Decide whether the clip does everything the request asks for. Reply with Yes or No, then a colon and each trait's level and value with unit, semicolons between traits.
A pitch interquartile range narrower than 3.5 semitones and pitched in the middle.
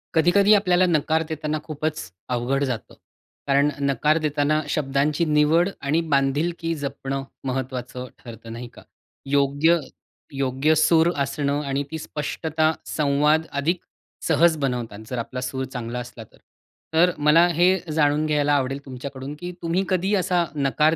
Yes: average, 3.0 semitones; medium, 150 Hz